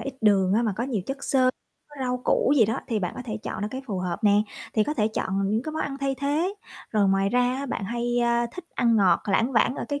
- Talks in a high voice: Yes, high, 235 Hz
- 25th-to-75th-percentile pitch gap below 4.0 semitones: No, average, 4.3 semitones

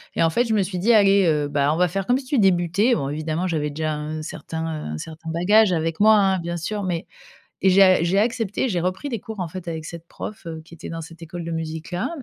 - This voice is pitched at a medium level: Yes, medium, 175 Hz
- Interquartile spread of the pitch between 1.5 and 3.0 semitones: No, average, 3.5 semitones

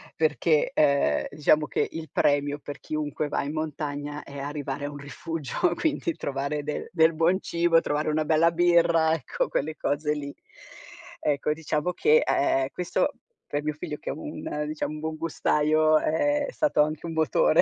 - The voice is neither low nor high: Yes, medium, 155 Hz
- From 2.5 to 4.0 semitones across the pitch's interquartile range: No, narrow, 2.0 semitones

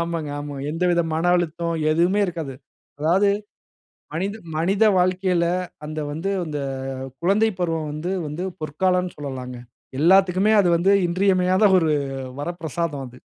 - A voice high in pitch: No, medium, 170 Hz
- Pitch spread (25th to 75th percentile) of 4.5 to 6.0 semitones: No, average, 3.0 semitones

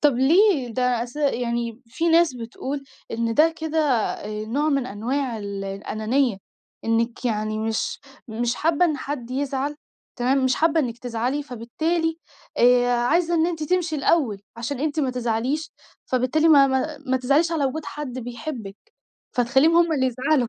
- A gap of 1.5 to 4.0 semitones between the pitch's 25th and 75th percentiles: No, average, 4.5 semitones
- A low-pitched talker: No, very high, 260 Hz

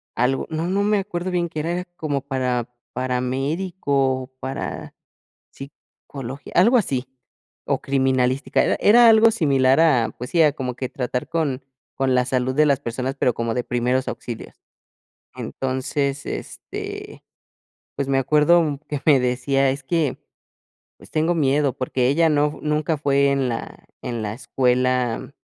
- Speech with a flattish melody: No, average, 3.3 semitones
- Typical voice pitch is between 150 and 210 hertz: No, low, 135 Hz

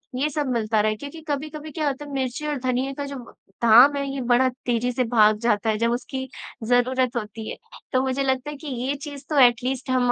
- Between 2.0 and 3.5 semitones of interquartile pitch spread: Yes, average, 2.8 semitones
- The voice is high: Yes, very high, 260 Hz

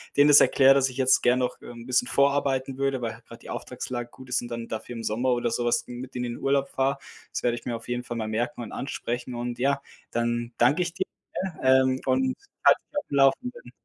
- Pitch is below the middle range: Yes, low, 125 Hz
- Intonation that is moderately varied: No, narrow, 2.3 semitones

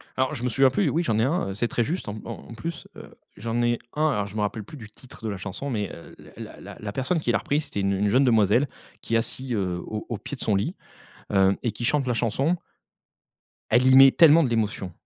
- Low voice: Yes, low, 120 Hz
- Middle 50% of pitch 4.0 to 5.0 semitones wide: Yes, average, 4.6 semitones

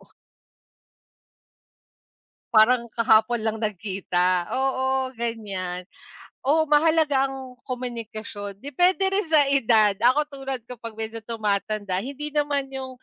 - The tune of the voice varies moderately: Yes, average, 4.0 semitones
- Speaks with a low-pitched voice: No, high, 245 Hz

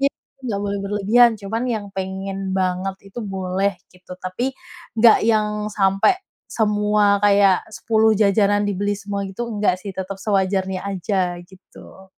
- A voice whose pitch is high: Yes, high, 200 Hz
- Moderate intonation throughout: No, narrow, 1.7 semitones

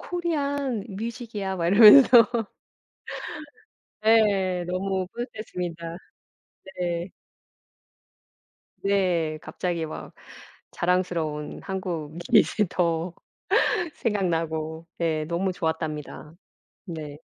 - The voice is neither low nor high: Yes, medium, 180 Hz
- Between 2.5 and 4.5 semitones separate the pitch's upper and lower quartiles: Yes, average, 3.9 semitones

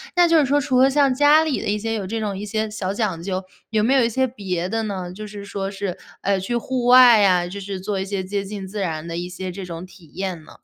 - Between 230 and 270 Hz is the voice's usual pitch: No, high, 200 Hz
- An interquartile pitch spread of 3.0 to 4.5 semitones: Yes, average, 3.8 semitones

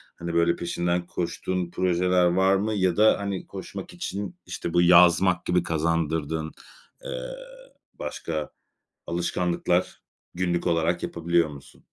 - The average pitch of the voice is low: Yes, very low, 85 Hz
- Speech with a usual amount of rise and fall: No, narrow, 1.6 semitones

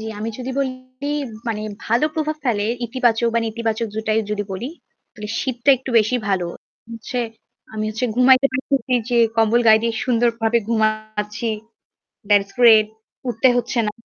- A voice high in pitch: Yes, high, 230 Hz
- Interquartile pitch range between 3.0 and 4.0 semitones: No, narrow, 2.4 semitones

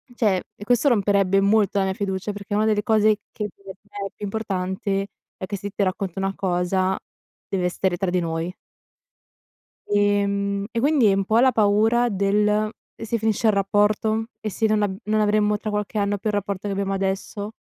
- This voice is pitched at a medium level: No, high, 205 Hz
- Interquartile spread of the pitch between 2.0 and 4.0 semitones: No, narrow, 1.6 semitones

